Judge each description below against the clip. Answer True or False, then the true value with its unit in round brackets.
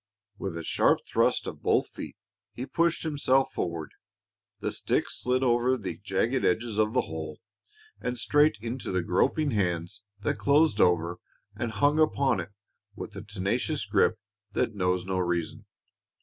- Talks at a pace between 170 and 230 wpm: False (155 wpm)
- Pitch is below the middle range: True (110 Hz)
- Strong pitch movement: True (6.4 semitones)